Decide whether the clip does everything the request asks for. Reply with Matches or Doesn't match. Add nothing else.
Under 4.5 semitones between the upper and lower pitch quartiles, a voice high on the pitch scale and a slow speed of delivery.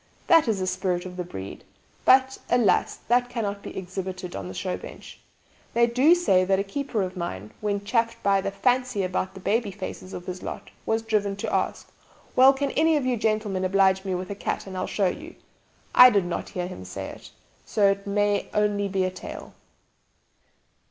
Doesn't match